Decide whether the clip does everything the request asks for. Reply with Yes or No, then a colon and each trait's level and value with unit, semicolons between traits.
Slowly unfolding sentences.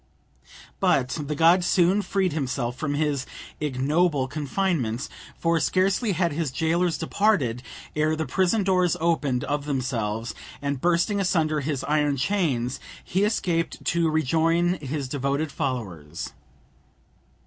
Yes: slow, 125 wpm